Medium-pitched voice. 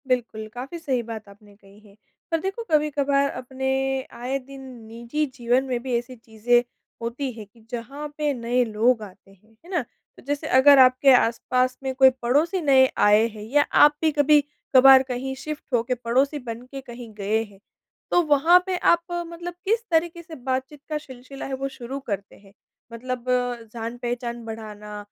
No: very high, 255 Hz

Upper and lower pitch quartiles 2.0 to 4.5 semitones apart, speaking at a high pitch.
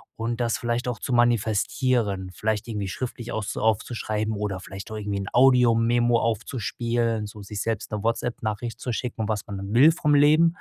No: narrow, 2.4 semitones; low, 115 Hz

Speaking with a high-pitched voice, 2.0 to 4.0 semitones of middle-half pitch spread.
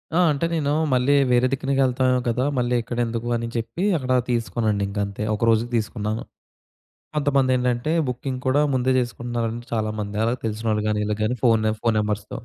No: low, 120 Hz; average, 2.7 semitones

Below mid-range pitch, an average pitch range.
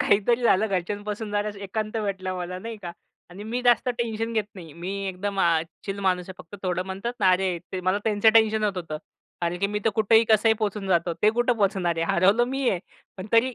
No: high, 200 Hz; average, 3.1 semitones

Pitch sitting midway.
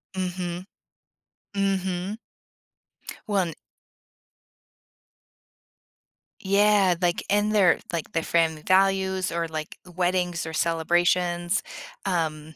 Yes: medium, 180 Hz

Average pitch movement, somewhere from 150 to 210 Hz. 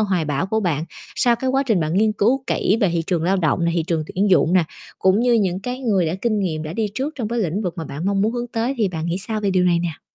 Yes: average, 4.8 semitones; high, 195 Hz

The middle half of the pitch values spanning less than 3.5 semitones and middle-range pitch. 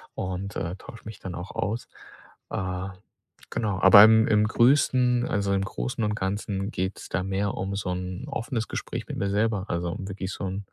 No: narrow, 2.6 semitones; low, 100 Hz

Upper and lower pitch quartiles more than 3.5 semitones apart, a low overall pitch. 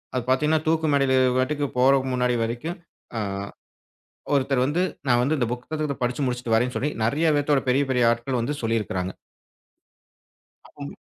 No: average, 3.1 semitones; low, 130 Hz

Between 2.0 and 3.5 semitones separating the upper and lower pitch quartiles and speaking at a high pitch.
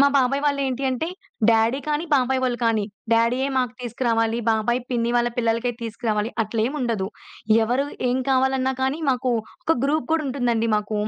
Yes: narrow, 2.6 semitones; high, 245 Hz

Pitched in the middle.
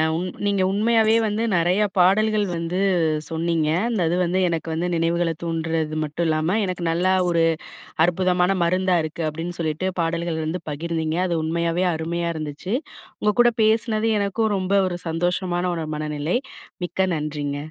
Yes: medium, 170 Hz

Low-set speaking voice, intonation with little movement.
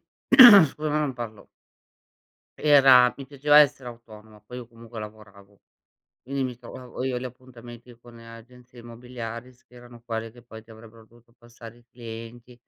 Yes: low, 120 Hz; narrow, 1.8 semitones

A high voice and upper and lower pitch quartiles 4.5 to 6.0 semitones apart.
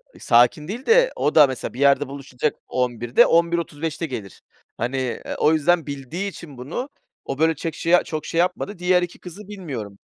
No: medium, 155 Hz; average, 5.0 semitones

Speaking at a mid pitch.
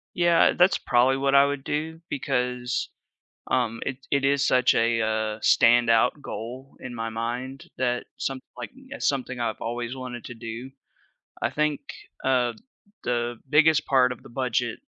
No: low, 125 Hz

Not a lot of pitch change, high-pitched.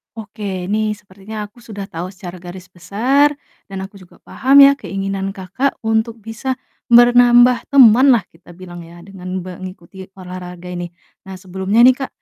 No: average, 4.2 semitones; high, 195 Hz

